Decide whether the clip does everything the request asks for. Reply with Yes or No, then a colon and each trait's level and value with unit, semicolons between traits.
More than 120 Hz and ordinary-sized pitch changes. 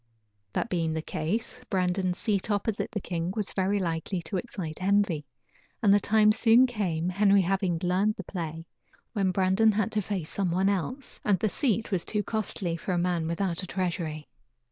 Yes: high, 190 Hz; average, 3.2 semitones